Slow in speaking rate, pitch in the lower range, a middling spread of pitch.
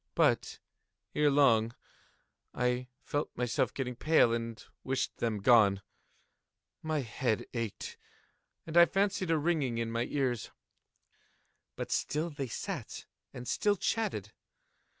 Yes: slow, 120 wpm; low, 125 Hz; average, 5.0 semitones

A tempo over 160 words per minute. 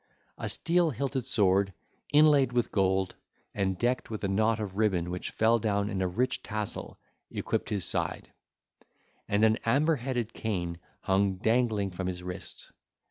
No: average, 155 wpm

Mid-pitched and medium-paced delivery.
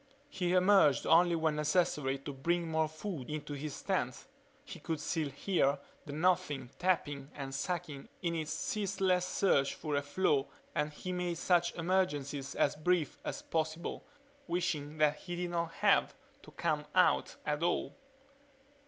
Yes: medium, 160 Hz; average, 155 wpm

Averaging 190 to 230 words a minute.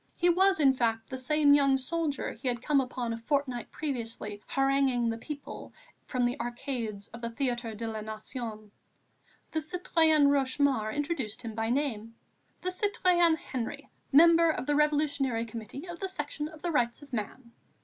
No: average, 170 wpm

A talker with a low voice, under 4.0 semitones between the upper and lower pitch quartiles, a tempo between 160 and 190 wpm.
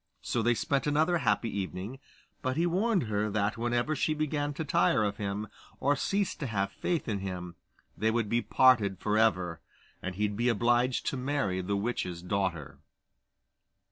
No: low, 115 Hz; wide, 5.6 semitones; average, 170 wpm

